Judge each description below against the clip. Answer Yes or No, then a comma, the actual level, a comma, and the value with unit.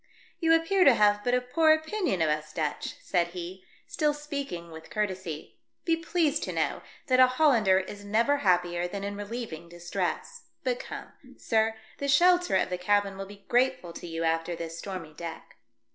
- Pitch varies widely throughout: Yes, wide, 8.5 semitones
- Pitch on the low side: No, high, 205 Hz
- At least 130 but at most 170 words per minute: No, average, 185 wpm